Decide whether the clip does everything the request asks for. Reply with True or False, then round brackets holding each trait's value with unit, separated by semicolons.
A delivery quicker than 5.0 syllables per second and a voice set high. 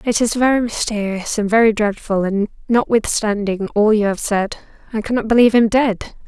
True (5.2 syllables/s; 215 Hz)